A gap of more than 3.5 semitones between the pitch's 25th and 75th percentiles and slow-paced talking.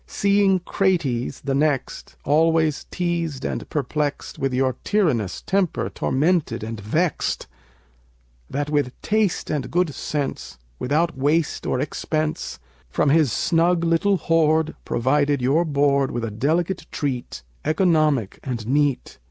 Yes: average, 4.0 semitones; slow, 125 wpm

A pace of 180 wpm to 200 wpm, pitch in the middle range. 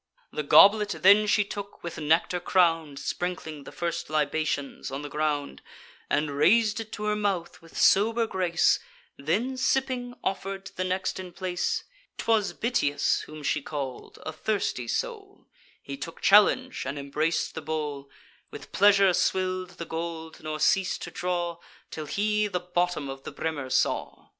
No: average, 160 wpm; medium, 175 Hz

